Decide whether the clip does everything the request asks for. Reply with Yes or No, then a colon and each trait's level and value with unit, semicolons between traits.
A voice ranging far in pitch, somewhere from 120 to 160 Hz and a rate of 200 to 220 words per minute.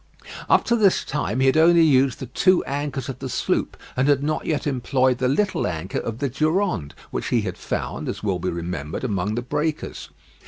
Yes: wide, 5.7 semitones; low, 135 Hz; fast, 205 wpm